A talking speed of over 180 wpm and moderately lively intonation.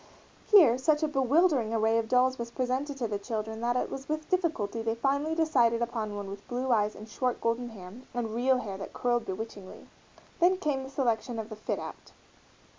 Yes: average, 200 wpm; average, 3.5 semitones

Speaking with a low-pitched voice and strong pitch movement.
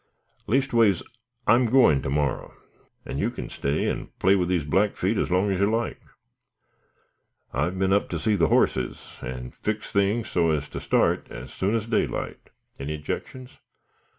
Yes: very low, 95 Hz; wide, 6.3 semitones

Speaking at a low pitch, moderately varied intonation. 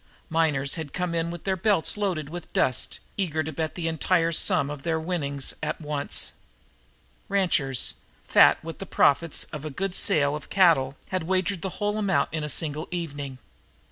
No: medium, 160 Hz; average, 3.5 semitones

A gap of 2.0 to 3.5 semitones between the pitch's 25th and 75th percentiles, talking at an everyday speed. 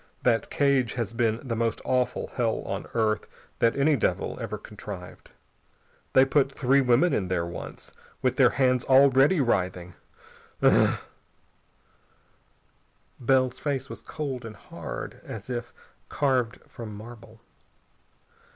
No: average, 3.2 semitones; slow, 125 wpm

